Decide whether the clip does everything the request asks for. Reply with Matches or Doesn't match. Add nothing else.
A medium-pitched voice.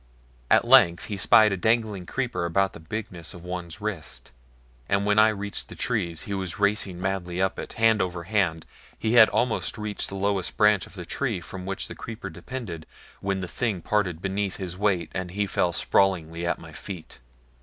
Doesn't match